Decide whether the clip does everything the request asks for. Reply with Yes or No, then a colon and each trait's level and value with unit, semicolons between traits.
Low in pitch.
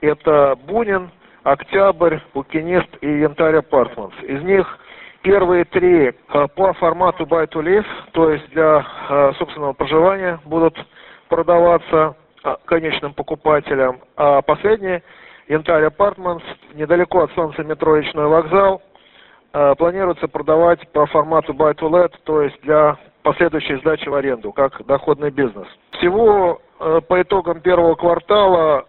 No: medium, 160 Hz